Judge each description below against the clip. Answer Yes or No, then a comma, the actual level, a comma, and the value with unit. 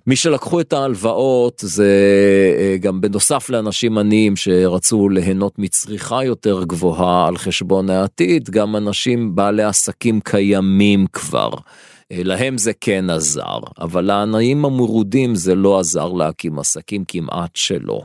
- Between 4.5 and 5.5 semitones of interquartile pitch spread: No, average, 3.5 semitones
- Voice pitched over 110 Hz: No, low, 100 Hz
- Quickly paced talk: No, average, 125 wpm